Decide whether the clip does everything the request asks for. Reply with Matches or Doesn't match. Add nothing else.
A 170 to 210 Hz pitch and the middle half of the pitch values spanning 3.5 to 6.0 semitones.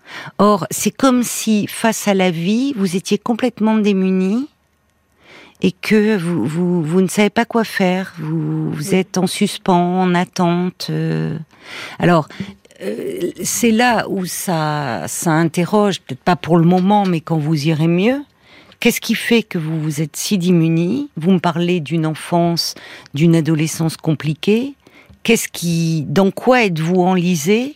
Matches